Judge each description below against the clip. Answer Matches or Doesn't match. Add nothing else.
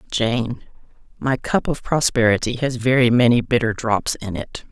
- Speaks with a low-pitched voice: Matches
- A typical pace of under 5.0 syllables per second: Matches